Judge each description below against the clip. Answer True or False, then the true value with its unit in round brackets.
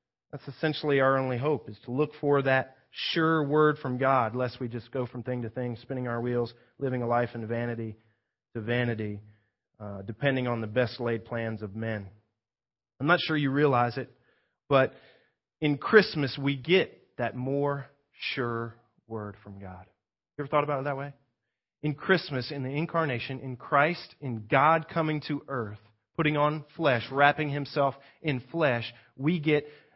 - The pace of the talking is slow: False (170 wpm)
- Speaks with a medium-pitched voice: False (130 Hz)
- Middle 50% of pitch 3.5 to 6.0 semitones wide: True (3.9 semitones)